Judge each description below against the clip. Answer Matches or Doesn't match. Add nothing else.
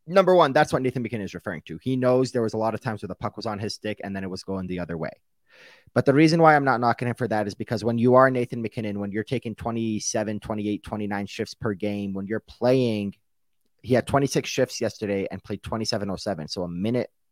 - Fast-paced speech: Matches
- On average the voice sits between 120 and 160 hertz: Doesn't match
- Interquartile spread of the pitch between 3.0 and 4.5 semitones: Matches